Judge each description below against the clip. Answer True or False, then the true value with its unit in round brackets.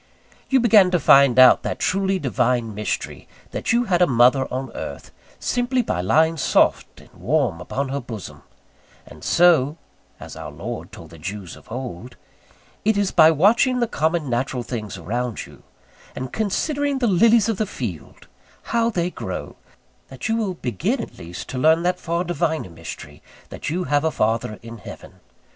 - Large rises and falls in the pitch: True (8.1 semitones)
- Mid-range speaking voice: True (150 Hz)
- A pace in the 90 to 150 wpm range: False (175 wpm)